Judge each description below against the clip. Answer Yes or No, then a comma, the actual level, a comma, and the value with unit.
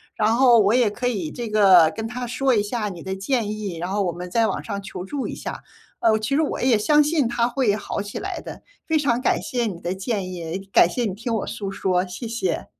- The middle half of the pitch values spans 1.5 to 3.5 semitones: No, average, 4.2 semitones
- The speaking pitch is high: Yes, high, 215 Hz